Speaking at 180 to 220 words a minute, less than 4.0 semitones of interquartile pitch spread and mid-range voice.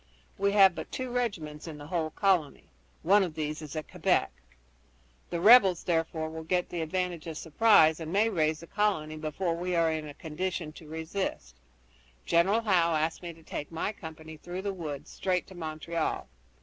Yes: average, 185 wpm; average, 3.1 semitones; medium, 165 Hz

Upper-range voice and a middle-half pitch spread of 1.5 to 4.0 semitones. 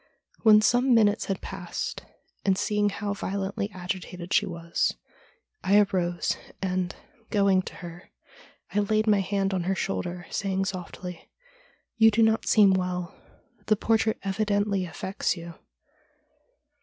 Yes: high, 195 Hz; narrow, 2.4 semitones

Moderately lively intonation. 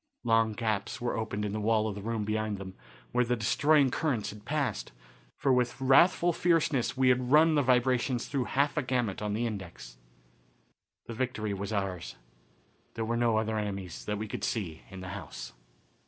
Yes: average, 3.7 semitones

